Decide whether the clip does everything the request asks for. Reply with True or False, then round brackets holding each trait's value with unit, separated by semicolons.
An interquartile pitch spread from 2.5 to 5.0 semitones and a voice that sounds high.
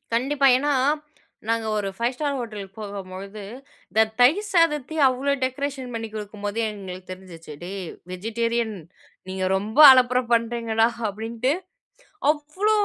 True (4.6 semitones; 230 Hz)